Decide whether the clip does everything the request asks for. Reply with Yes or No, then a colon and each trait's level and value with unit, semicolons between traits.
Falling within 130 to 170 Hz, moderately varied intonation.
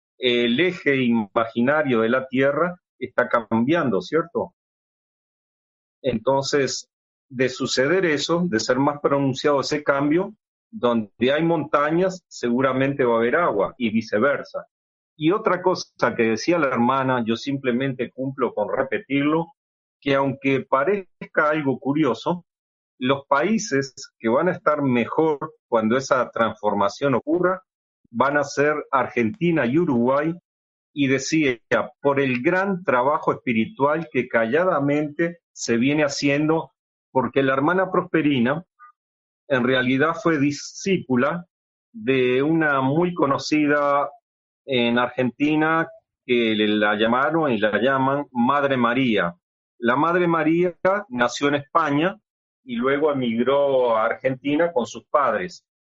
Yes: medium, 140 Hz; average, 4.8 semitones